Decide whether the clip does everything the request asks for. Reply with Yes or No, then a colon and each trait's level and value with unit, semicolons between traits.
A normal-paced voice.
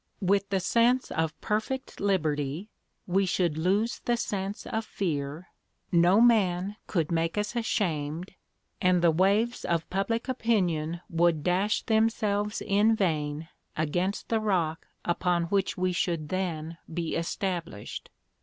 No: slow, 130 wpm